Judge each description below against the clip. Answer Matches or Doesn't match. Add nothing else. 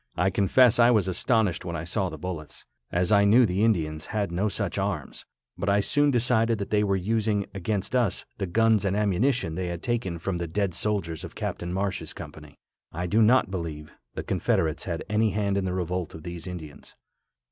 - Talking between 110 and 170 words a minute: Doesn't match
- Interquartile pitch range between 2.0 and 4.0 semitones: Matches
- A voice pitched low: Matches